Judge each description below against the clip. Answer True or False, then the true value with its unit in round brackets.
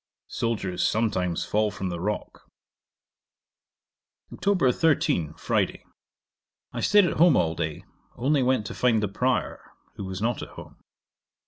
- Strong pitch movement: True (5.7 semitones)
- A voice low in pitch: True (110 Hz)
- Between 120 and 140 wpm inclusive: True (135 wpm)